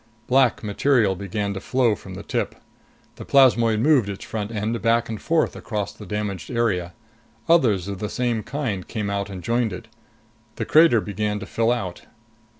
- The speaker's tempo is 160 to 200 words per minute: Yes, average, 175 wpm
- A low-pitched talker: Yes, low, 110 Hz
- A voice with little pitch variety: No, average, 3.1 semitones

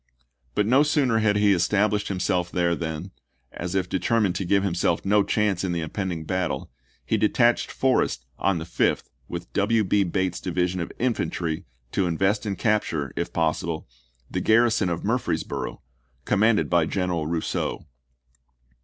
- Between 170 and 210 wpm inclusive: No, average, 155 wpm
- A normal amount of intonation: Yes, average, 3.4 semitones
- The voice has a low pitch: Yes, very low, 95 Hz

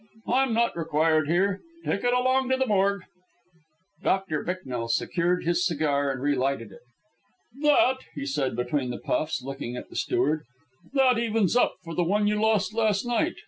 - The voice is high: No, medium, 180 Hz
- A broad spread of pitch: Yes, wide, 7.7 semitones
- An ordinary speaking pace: Yes, average, 170 wpm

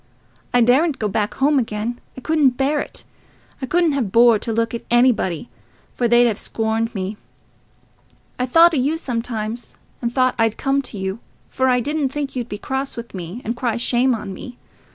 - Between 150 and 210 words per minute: Yes, average, 190 wpm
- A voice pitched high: Yes, high, 240 Hz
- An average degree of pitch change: Yes, average, 3.1 semitones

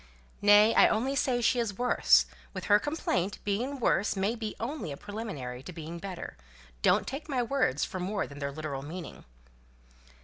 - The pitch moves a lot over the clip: Yes, wide, 6.6 semitones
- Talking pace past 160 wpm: Yes, average, 175 wpm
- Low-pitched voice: No, high, 205 Hz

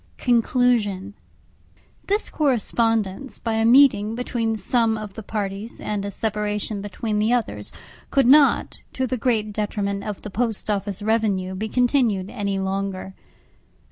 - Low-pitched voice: No, high, 215 Hz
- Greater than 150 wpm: No, average, 140 wpm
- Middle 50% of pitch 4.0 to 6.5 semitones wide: No, average, 3.0 semitones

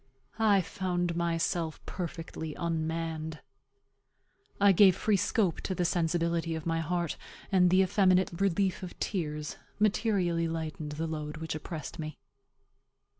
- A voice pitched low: No, medium, 170 Hz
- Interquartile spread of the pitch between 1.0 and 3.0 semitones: Yes, narrow, 2.5 semitones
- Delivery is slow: Yes, slow, 125 wpm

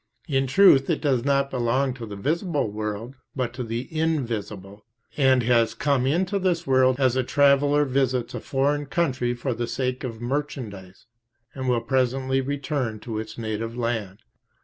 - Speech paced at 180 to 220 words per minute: No, average, 165 wpm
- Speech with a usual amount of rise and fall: Yes, average, 3.3 semitones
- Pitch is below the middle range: Yes, low, 130 Hz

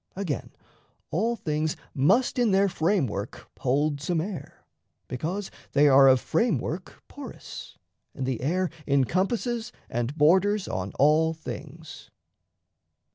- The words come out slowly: Yes, slow, 115 wpm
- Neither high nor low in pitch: Yes, medium, 160 Hz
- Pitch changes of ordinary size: No, wide, 6.0 semitones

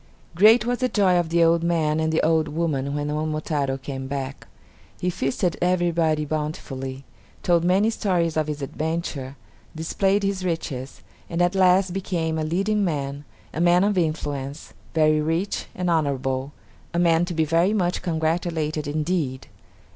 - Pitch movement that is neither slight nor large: Yes, average, 3.1 semitones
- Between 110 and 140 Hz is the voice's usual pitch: No, medium, 160 Hz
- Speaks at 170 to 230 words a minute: No, average, 155 wpm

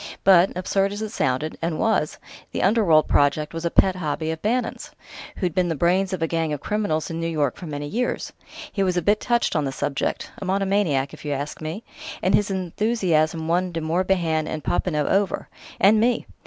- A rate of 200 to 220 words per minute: Yes, fast, 205 wpm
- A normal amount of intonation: Yes, average, 4.0 semitones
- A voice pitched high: No, medium, 175 Hz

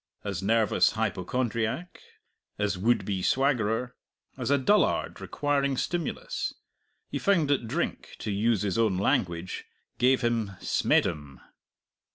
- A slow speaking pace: Yes, slow, 120 wpm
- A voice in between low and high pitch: No, low, 115 Hz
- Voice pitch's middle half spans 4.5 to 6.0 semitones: Yes, average, 5.2 semitones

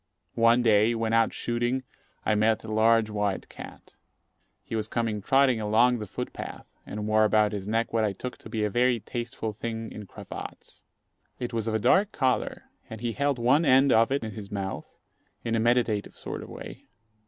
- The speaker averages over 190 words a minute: Yes, average, 200 wpm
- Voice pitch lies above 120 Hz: No, low, 115 Hz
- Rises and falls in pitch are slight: Yes, narrow, 2.1 semitones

